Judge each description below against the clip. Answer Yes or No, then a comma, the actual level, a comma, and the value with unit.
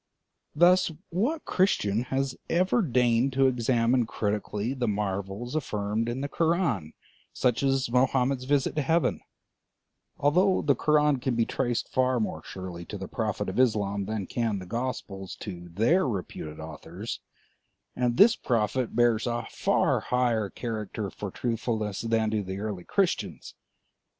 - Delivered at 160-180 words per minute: No, average, 145 wpm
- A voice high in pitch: No, low, 120 Hz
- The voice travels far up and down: No, average, 4.4 semitones